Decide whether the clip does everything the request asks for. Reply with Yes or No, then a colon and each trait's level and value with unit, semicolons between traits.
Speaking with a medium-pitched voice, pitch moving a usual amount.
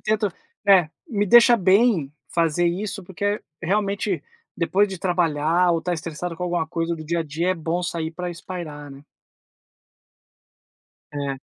Yes: medium, 175 Hz; average, 3.2 semitones